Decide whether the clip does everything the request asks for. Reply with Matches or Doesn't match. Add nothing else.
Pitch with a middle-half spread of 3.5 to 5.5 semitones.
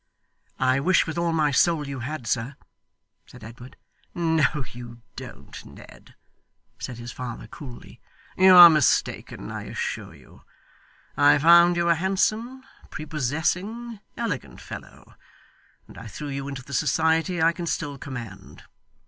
Matches